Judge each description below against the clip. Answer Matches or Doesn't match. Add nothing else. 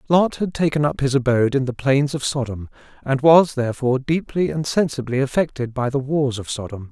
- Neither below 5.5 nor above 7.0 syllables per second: Matches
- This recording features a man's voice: Matches